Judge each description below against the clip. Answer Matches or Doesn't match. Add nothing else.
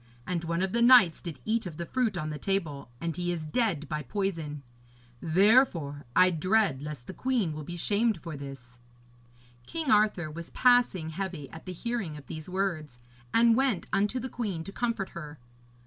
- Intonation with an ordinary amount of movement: Doesn't match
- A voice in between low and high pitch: Matches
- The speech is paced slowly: Doesn't match